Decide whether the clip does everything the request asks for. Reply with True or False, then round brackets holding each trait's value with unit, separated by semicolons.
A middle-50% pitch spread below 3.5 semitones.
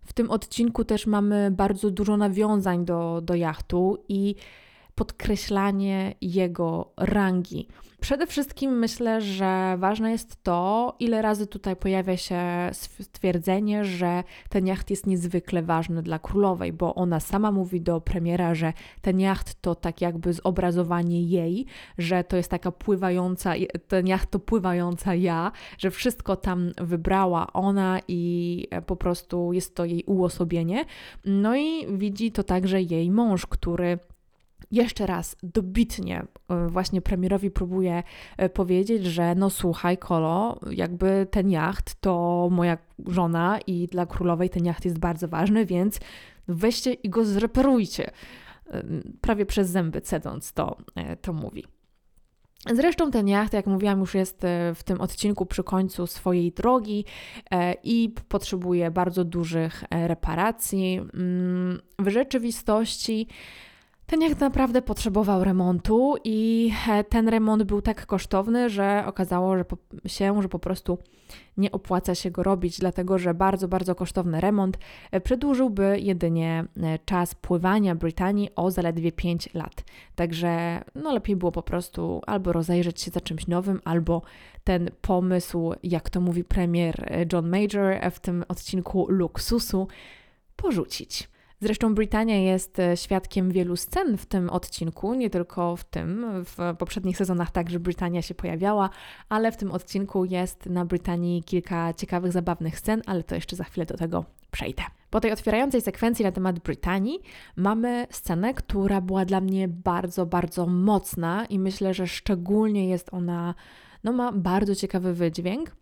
True (2.6 semitones)